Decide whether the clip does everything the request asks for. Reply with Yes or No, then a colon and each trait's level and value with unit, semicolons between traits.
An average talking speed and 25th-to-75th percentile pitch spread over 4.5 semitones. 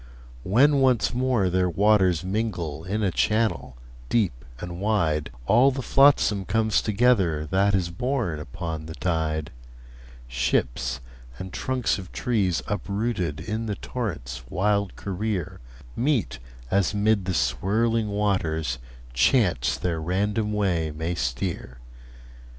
No: slow, 120 wpm; average, 5.2 semitones